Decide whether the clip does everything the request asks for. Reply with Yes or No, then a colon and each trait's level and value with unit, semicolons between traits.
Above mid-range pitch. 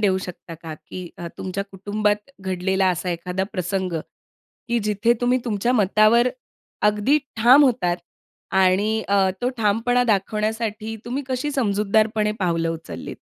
Yes: high, 205 Hz